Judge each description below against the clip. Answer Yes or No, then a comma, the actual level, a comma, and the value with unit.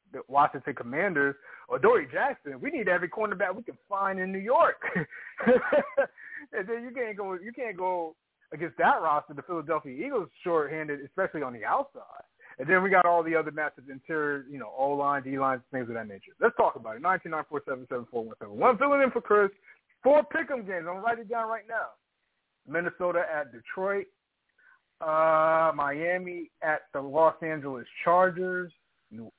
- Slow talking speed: No, average, 190 wpm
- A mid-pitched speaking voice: Yes, medium, 175 Hz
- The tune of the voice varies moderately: No, wide, 7.0 semitones